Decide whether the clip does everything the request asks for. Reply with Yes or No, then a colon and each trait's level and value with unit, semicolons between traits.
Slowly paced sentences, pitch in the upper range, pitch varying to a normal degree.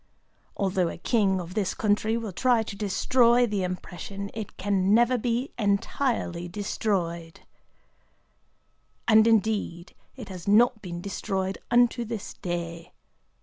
Yes: slow, 125 wpm; high, 205 Hz; average, 3.8 semitones